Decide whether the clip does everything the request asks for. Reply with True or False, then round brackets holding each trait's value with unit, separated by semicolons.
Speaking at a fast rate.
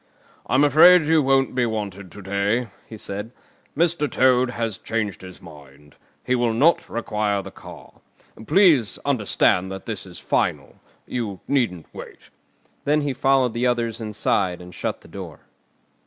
False (155 wpm)